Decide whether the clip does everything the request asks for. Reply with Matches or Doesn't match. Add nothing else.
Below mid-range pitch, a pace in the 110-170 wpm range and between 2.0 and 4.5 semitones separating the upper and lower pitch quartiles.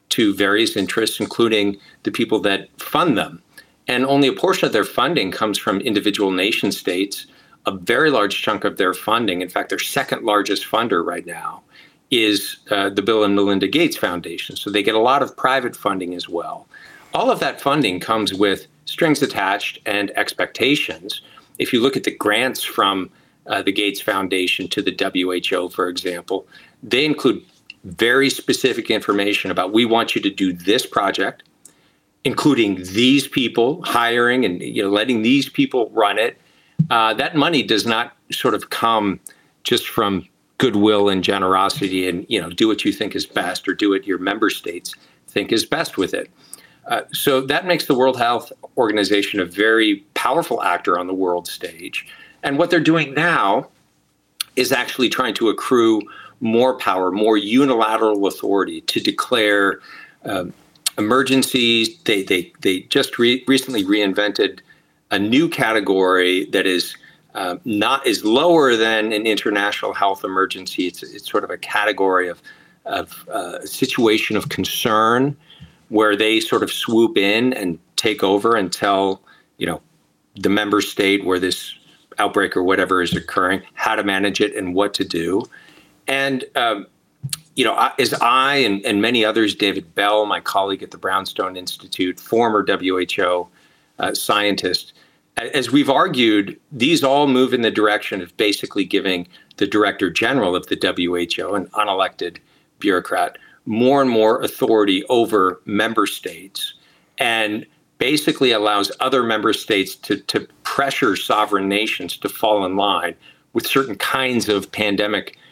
Matches